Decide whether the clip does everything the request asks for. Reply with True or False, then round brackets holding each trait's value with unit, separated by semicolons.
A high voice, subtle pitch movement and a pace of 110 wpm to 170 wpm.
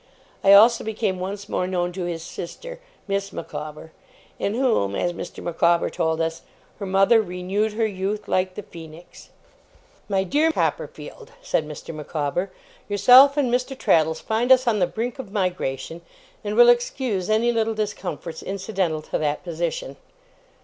False (195 Hz; 4.8 semitones; 155 wpm)